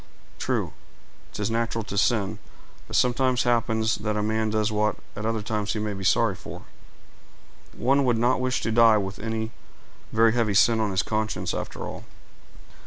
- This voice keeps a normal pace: Yes, average, 175 wpm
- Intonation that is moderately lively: No, narrow, 1.7 semitones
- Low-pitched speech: Yes, low, 110 Hz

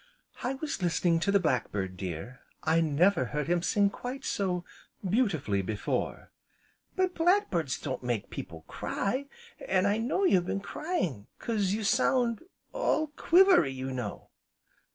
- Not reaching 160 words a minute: Yes, average, 150 wpm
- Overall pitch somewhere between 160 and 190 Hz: Yes, medium, 185 Hz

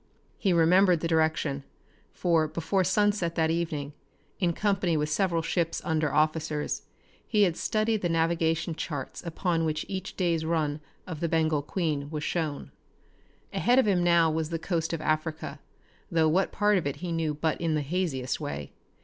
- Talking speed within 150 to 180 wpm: Yes, average, 170 wpm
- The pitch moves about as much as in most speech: No, narrow, 2.3 semitones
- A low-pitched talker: No, medium, 165 Hz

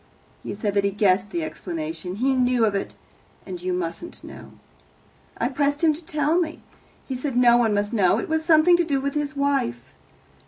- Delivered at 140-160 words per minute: No, average, 200 wpm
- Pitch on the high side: Yes, very high, 255 Hz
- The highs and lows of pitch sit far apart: Yes, wide, 7.2 semitones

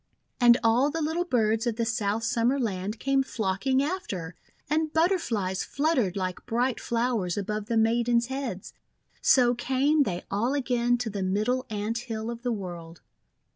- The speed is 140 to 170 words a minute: Yes, average, 160 wpm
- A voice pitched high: Yes, high, 235 Hz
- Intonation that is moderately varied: Yes, average, 4.1 semitones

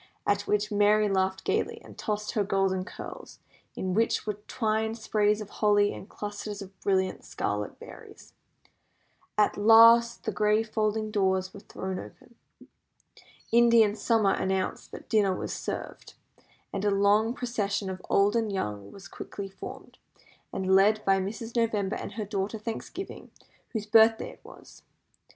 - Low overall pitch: No, high, 205 Hz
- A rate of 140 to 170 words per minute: Yes, average, 150 wpm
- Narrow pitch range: Yes, narrow, 2.2 semitones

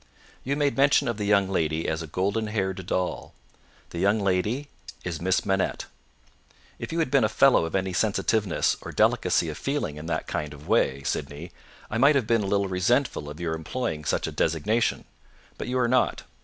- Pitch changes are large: Yes, wide, 6.2 semitones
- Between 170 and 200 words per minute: Yes, average, 195 wpm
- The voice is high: No, low, 100 Hz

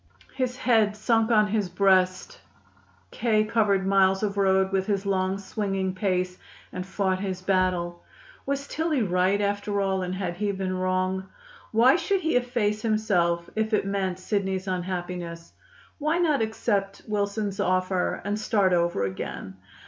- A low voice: No, high, 195 Hz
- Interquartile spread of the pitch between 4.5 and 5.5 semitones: No, narrow, 2.5 semitones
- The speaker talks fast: No, average, 150 wpm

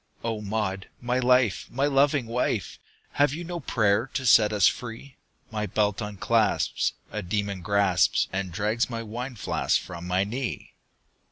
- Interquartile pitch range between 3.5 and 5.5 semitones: Yes, average, 3.8 semitones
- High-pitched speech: No, low, 110 Hz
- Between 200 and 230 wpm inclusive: No, average, 155 wpm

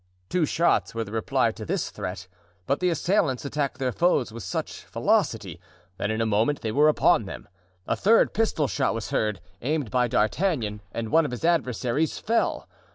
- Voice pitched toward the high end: No, low, 130 Hz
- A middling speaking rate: Yes, average, 185 wpm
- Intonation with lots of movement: Yes, wide, 6.2 semitones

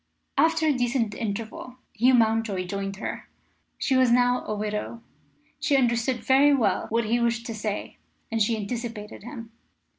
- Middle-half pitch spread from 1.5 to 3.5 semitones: Yes, average, 2.7 semitones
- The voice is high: Yes, high, 230 Hz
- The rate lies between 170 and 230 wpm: No, average, 155 wpm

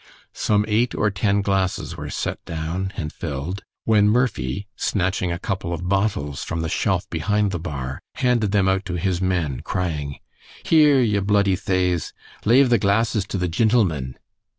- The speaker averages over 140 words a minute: Yes, average, 165 wpm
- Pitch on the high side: No, very low, 95 Hz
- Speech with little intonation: No, average, 3.5 semitones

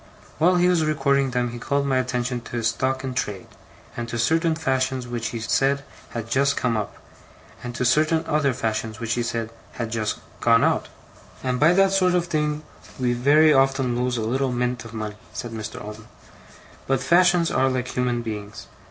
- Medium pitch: No, low, 125 Hz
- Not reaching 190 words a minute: No, average, 195 wpm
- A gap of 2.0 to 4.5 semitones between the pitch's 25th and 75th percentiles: Yes, average, 3.6 semitones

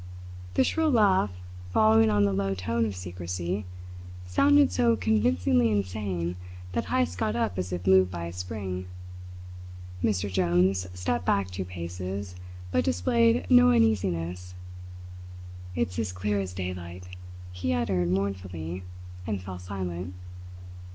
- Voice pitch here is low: Yes, very low, 95 Hz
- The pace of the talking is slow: Yes, slow, 130 wpm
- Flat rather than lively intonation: Yes, narrow, 2.2 semitones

